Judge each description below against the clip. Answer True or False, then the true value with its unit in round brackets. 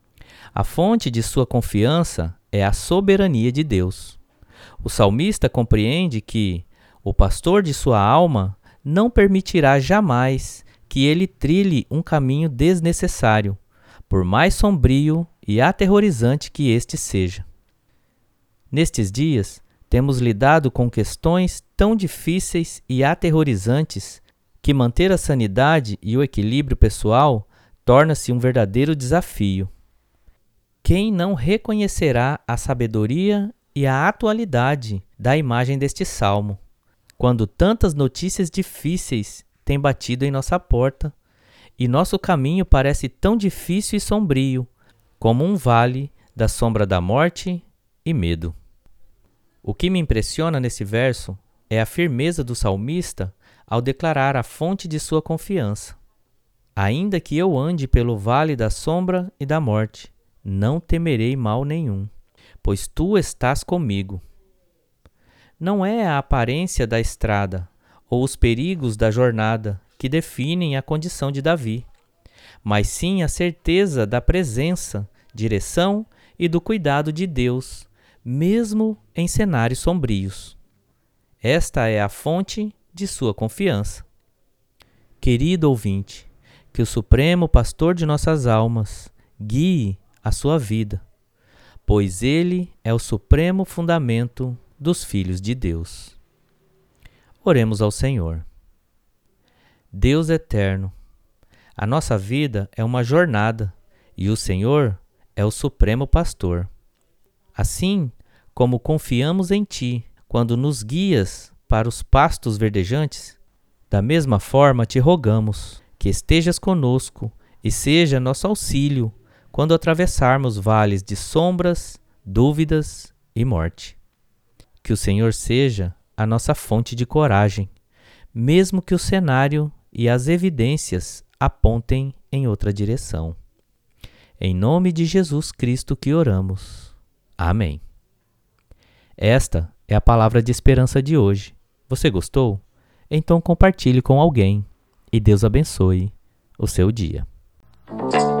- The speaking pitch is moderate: False (120 Hz)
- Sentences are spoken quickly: False (120 wpm)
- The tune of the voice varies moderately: False (7.3 semitones)